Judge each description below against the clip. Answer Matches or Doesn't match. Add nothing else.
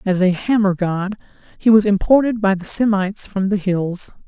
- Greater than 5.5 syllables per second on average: Doesn't match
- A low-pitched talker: Doesn't match